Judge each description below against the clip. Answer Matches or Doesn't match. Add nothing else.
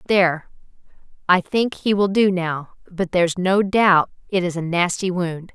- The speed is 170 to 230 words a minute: Matches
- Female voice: Matches